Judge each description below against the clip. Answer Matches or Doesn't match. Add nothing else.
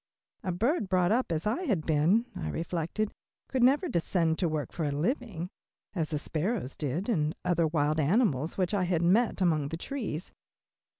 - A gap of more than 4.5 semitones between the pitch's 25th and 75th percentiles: Matches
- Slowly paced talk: Doesn't match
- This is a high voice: Doesn't match